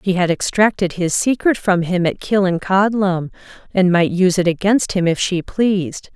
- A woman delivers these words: Yes, female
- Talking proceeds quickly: No, average, 175 wpm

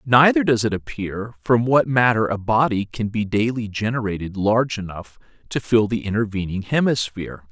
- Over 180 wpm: No, average, 160 wpm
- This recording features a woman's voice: No, male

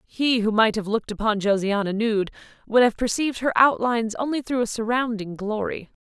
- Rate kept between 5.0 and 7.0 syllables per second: Yes, 5.5 syllables/s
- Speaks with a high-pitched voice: Yes, high, 225 Hz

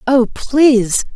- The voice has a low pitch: No, very high, 250 Hz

